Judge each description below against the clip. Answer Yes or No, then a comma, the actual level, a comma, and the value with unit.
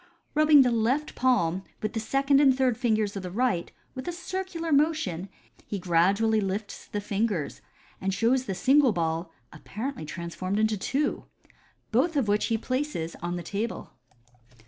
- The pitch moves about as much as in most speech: No, wide, 6.3 semitones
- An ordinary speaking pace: Yes, average, 160 wpm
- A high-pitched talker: Yes, high, 220 Hz